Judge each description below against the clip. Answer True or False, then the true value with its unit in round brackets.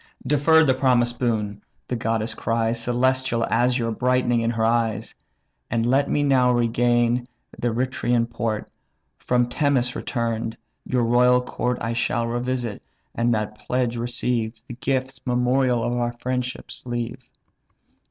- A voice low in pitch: True (120 Hz)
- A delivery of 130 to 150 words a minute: True (135 wpm)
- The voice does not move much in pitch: True (1.5 semitones)